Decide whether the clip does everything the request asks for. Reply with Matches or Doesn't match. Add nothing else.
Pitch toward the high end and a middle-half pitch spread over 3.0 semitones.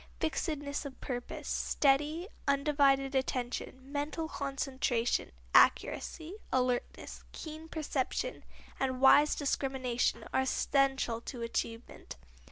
Doesn't match